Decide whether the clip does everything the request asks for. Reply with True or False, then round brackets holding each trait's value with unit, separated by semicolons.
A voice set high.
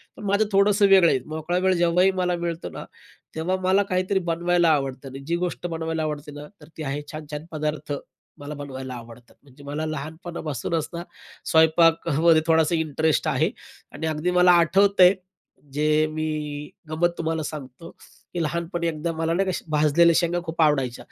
False (160 Hz)